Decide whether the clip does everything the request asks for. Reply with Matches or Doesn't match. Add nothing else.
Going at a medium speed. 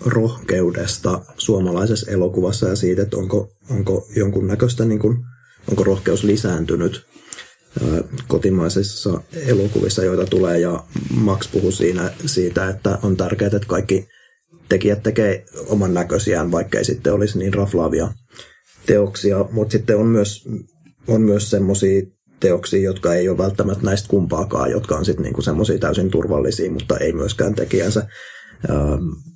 Matches